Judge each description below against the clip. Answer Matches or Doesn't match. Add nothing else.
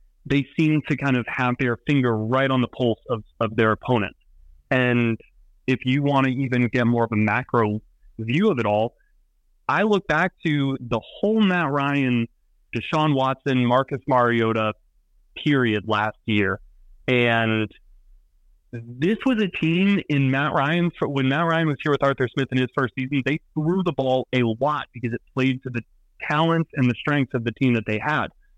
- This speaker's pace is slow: Doesn't match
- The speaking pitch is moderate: Doesn't match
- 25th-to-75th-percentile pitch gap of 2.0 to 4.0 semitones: Doesn't match